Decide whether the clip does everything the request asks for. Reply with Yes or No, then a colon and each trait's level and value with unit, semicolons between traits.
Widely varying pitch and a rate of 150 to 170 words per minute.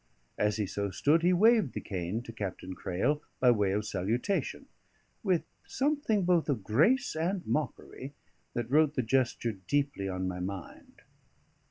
Yes: wide, 8.6 semitones; average, 155 wpm